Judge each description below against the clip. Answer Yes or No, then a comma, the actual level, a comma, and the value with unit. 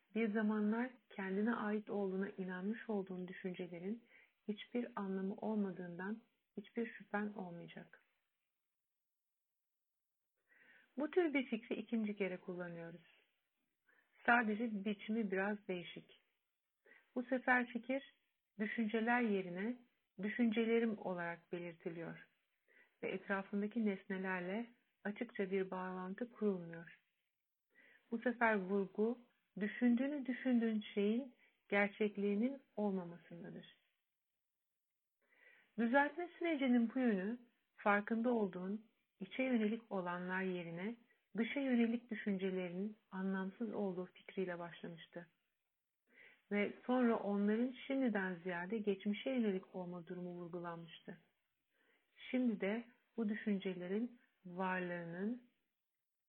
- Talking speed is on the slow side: Yes, slow, 85 wpm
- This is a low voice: No, high, 210 Hz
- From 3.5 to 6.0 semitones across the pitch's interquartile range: Yes, average, 4.0 semitones